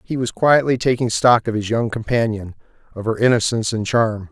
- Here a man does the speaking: Yes, male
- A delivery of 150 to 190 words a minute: Yes, average, 180 wpm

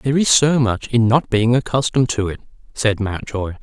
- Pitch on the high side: No, low, 120 Hz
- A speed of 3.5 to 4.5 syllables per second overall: No, 5.4 syllables/s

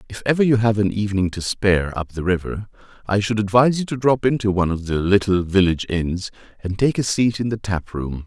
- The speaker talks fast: Yes, fast, 230 wpm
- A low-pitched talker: Yes, low, 100 Hz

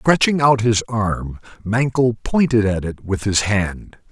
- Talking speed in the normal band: Yes, average, 160 wpm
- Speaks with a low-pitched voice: Yes, low, 110 Hz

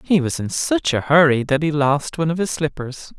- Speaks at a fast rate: Yes, fast, 245 wpm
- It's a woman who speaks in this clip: No, male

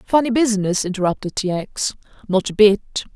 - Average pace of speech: Yes, average, 150 wpm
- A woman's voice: Yes, female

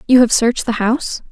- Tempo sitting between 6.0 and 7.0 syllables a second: Yes, 6.4 syllables/s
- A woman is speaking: Yes, female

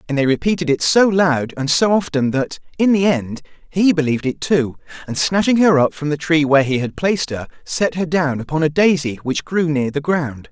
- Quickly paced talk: Yes, fast, 230 wpm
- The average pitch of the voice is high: No, medium, 155 Hz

